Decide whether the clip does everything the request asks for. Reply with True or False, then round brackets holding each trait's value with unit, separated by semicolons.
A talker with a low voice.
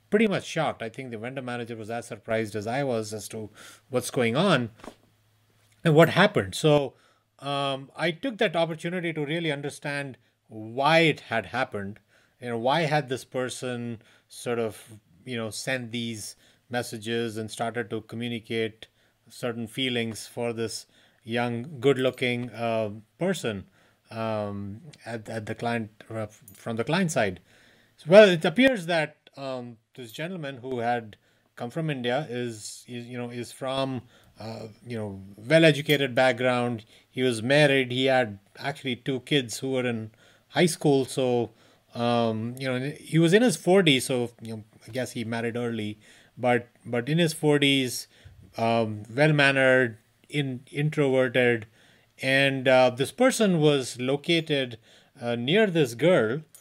True (125 Hz)